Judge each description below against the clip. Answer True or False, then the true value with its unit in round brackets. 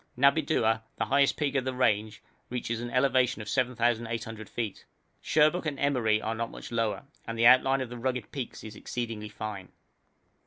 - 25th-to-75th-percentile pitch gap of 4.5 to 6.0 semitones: False (2.9 semitones)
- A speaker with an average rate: True (170 wpm)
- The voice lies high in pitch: False (120 Hz)